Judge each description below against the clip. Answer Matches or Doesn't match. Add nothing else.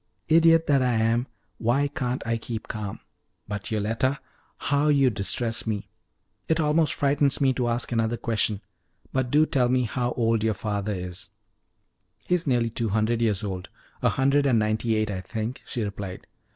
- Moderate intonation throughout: Matches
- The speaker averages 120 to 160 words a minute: Doesn't match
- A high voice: Doesn't match